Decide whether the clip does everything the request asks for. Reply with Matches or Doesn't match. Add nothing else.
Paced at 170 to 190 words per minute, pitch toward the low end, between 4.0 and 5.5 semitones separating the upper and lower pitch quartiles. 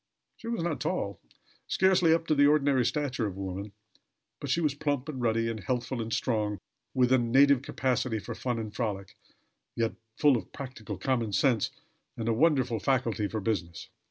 Matches